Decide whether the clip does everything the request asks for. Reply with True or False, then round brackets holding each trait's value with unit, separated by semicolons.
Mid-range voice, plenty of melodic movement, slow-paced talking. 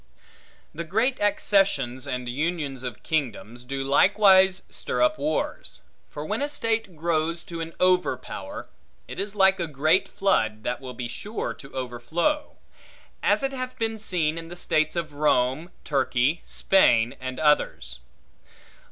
False (160 Hz; 6.8 semitones; 150 wpm)